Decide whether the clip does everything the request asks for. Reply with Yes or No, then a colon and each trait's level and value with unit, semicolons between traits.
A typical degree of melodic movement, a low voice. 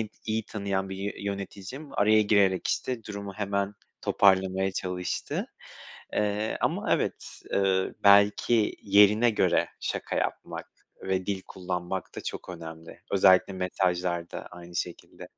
No: narrow, 1.8 semitones; low, 100 Hz